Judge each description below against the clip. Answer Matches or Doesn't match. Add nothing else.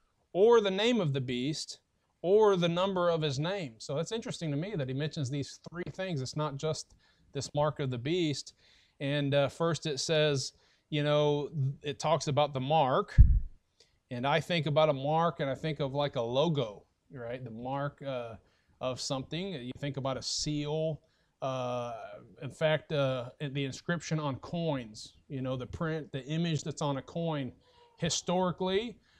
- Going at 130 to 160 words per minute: Doesn't match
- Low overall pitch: Doesn't match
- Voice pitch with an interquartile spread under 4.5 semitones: Matches